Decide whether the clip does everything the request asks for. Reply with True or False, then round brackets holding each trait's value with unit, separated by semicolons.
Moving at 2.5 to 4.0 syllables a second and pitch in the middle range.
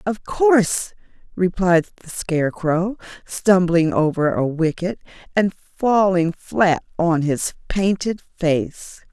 True (3.6 syllables/s; 180 Hz)